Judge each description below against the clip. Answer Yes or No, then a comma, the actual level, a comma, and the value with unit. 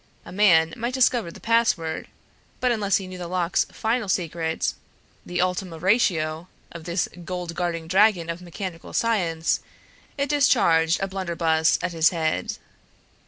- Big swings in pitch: No, average, 3.7 semitones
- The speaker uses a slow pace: No, average, 145 wpm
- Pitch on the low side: No, medium, 180 Hz